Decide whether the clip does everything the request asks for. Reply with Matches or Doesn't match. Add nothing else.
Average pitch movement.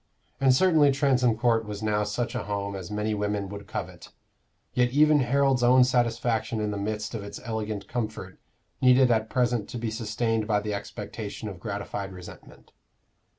Matches